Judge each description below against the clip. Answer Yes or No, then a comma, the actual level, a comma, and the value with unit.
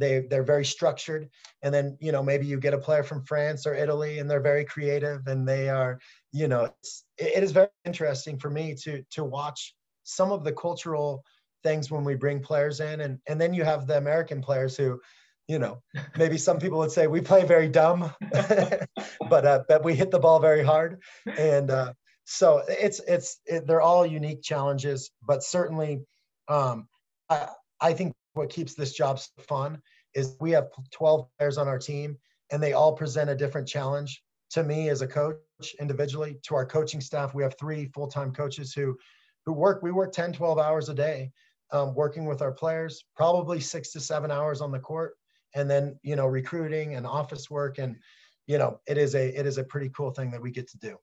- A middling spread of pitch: No, narrow, 2.1 semitones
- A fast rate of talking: Yes, fast, 205 wpm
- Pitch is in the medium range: Yes, medium, 150 Hz